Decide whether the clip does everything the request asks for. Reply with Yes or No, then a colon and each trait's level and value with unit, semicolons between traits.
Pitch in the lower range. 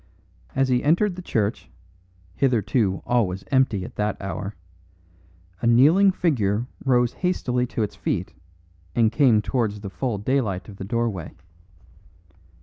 Yes: low, 115 Hz